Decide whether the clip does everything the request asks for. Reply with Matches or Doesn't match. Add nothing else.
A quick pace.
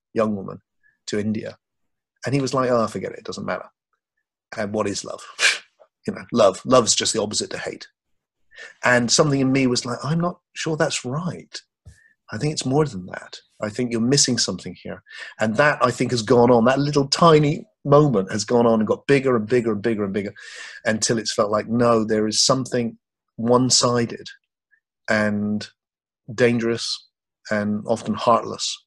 Doesn't match